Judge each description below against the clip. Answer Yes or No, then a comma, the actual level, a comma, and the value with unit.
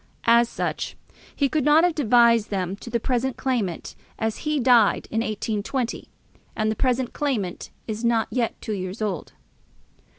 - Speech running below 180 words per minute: Yes, average, 160 wpm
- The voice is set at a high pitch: Yes, high, 235 Hz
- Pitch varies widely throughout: No, average, 3.3 semitones